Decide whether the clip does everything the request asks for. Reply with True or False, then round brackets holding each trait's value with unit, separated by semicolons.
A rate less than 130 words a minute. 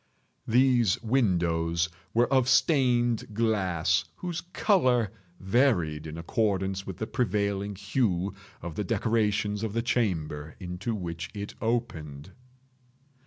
True (115 wpm)